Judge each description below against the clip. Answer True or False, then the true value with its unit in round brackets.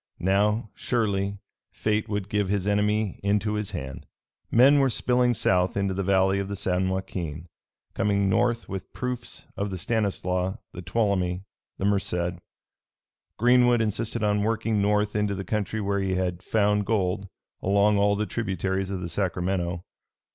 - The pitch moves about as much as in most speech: False (2.1 semitones)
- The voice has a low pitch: True (100 Hz)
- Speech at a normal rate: True (155 wpm)